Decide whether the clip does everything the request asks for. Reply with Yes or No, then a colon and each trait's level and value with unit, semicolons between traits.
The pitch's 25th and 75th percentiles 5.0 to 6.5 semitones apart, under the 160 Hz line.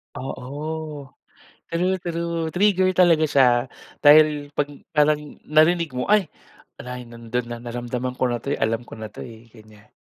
Yes: wide, 5.6 semitones; medium, 140 Hz